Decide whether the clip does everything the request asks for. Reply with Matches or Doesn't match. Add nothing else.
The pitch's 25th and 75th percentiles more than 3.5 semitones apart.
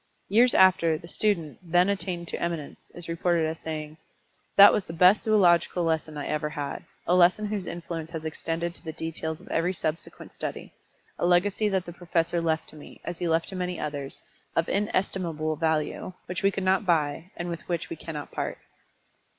Doesn't match